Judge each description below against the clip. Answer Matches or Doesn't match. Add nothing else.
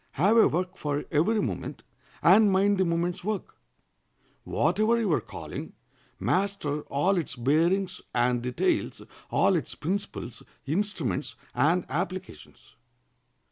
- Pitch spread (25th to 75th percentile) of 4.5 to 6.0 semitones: Matches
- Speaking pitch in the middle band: Matches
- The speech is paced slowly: Matches